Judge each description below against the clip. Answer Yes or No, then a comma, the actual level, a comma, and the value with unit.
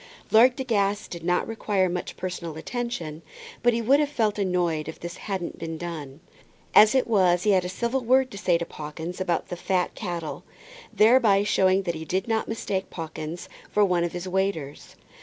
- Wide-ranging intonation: No, average, 4.2 semitones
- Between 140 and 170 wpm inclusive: No, average, 195 wpm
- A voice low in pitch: No, medium, 185 Hz